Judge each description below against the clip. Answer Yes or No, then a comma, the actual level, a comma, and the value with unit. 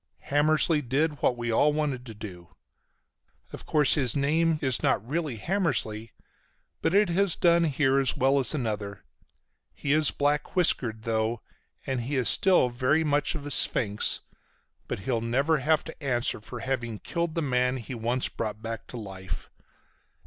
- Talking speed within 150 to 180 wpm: Yes, average, 165 wpm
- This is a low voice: Yes, low, 130 Hz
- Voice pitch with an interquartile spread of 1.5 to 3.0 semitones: No, average, 4.8 semitones